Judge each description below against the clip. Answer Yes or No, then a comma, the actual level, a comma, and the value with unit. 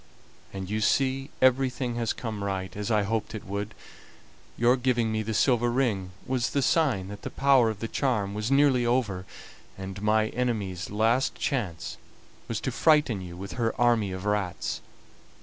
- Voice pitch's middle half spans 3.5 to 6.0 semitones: Yes, average, 3.9 semitones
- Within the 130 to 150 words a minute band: No, average, 170 wpm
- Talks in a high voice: No, low, 110 Hz